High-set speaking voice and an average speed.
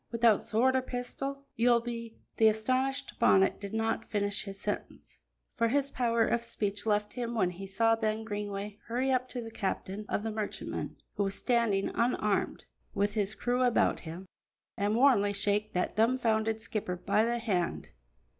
Yes: high, 220 Hz; average, 175 wpm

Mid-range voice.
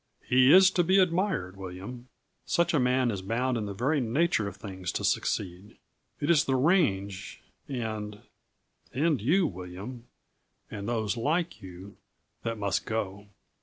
No: low, 115 Hz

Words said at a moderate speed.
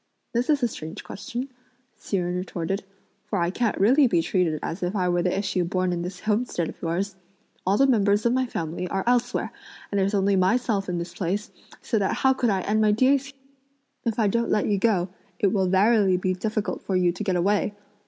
No: fast, 220 wpm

